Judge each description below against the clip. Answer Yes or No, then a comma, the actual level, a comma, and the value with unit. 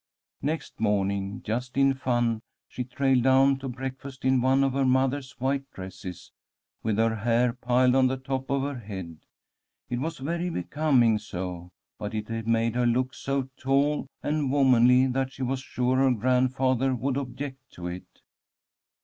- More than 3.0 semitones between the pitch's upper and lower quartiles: No, narrow, 2.6 semitones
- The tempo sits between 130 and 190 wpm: Yes, average, 160 wpm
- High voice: No, low, 130 Hz